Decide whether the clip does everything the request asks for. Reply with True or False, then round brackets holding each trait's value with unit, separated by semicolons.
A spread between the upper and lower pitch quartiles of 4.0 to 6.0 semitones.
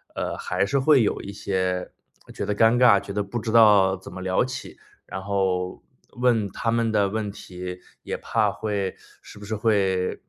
False (2.9 semitones)